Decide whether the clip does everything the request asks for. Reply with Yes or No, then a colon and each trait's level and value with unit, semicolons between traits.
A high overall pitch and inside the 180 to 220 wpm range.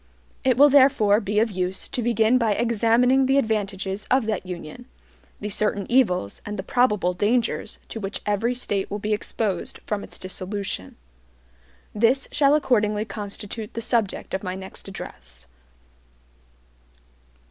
No: high, 210 Hz; average, 145 wpm